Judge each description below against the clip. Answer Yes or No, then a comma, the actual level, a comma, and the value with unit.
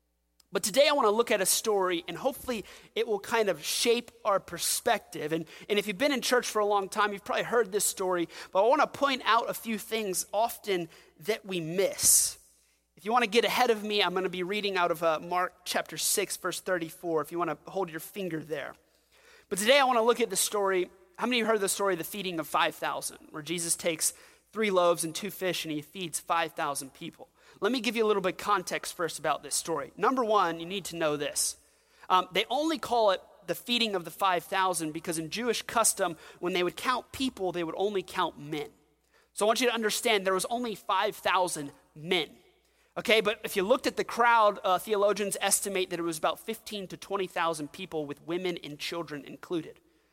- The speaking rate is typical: No, fast, 225 wpm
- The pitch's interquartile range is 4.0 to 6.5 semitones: Yes, average, 4.7 semitones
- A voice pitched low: No, high, 190 Hz